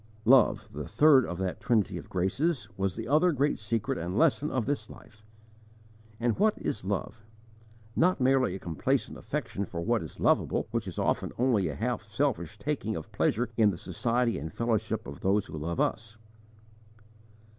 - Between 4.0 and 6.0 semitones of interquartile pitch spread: Yes, average, 5.0 semitones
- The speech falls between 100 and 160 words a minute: No, average, 175 wpm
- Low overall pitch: Yes, low, 110 Hz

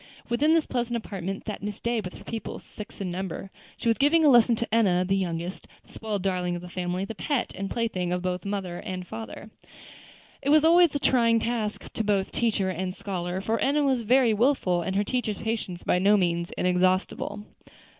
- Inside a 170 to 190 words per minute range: No, fast, 205 wpm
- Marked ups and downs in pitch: No, average, 4.3 semitones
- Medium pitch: No, high, 205 Hz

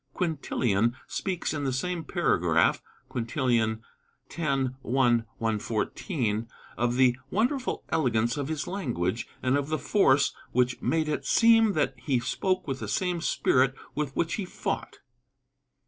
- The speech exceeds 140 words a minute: No, slow, 135 wpm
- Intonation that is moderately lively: No, wide, 5.9 semitones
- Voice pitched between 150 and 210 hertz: No, low, 135 Hz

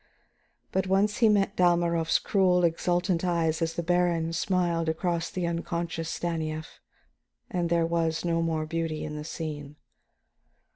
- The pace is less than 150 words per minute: Yes, average, 140 wpm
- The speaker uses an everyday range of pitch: No, narrow, 1.5 semitones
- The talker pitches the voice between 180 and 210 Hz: No, medium, 170 Hz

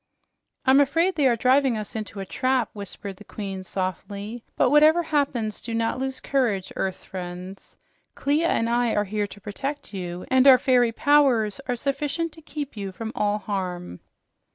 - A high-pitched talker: Yes, high, 230 Hz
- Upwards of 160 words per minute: Yes, average, 175 wpm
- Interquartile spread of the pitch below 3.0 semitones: No, wide, 5.5 semitones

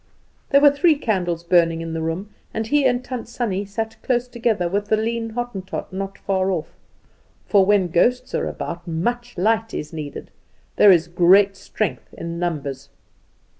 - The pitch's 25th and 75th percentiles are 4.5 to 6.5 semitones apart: Yes, average, 5.2 semitones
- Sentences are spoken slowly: No, average, 170 wpm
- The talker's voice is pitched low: No, high, 200 Hz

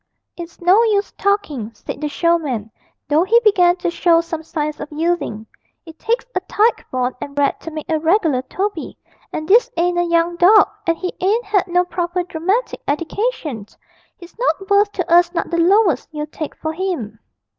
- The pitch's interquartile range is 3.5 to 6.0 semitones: Yes, average, 3.9 semitones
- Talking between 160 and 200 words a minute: Yes, average, 185 wpm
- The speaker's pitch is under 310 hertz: No, very high, 345 Hz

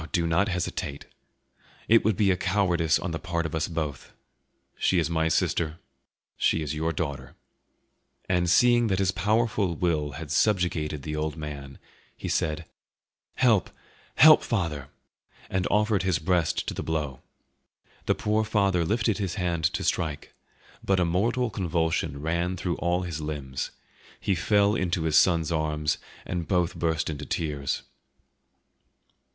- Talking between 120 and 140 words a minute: No, average, 155 wpm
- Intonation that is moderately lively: Yes, average, 3.6 semitones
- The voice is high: No, very low, 85 Hz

